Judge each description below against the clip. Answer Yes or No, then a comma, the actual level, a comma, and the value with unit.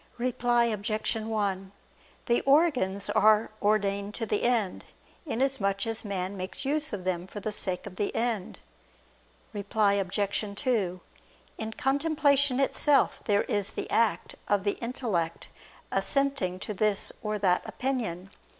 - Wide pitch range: No, average, 3.7 semitones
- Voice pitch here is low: No, high, 210 Hz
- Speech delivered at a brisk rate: No, slow, 135 wpm